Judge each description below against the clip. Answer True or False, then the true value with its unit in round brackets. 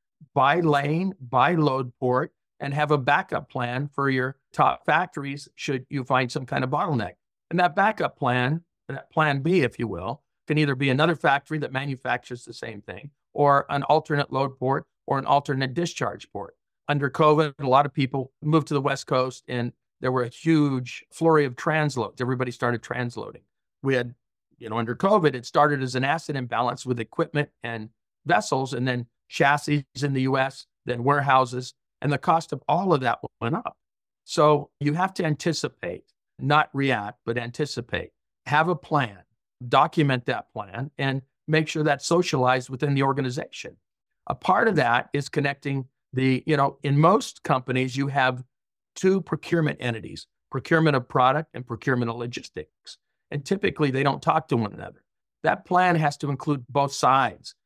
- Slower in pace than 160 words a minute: False (175 wpm)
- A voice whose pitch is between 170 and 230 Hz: False (140 Hz)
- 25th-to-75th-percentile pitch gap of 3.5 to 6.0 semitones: False (3.1 semitones)